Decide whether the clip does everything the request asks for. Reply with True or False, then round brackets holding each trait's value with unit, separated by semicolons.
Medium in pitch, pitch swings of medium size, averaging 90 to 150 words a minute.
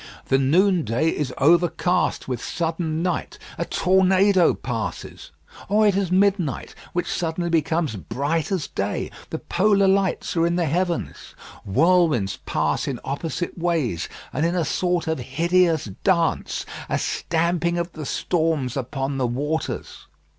True (165 Hz; 4.3 semitones; 140 wpm)